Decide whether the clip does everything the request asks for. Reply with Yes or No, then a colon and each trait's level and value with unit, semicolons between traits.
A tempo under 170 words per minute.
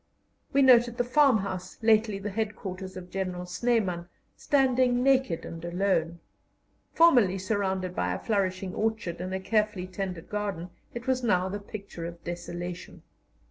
Yes: average, 140 wpm